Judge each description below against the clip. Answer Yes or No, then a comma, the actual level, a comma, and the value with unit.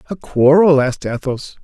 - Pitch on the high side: No, medium, 145 Hz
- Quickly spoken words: No, average, 145 wpm